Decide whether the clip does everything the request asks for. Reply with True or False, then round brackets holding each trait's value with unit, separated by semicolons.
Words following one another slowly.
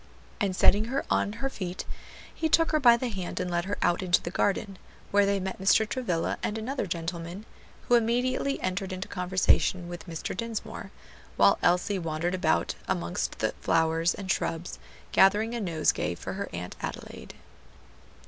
False (165 wpm)